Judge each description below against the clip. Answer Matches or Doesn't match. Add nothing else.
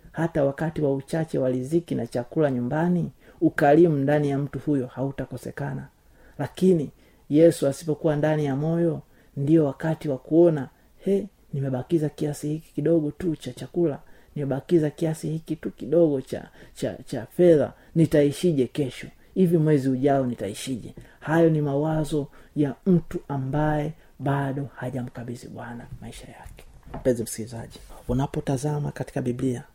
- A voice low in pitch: Doesn't match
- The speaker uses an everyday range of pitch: Matches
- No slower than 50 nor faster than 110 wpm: Doesn't match